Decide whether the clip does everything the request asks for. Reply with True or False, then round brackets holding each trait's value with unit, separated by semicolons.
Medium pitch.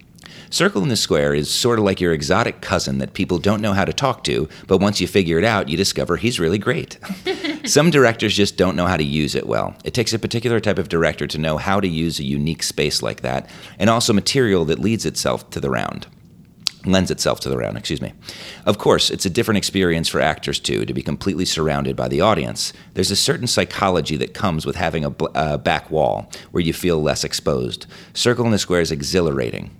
False (95 Hz)